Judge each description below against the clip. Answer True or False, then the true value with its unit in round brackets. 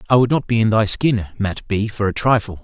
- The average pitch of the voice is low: True (110 Hz)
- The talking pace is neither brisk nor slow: False (275 wpm)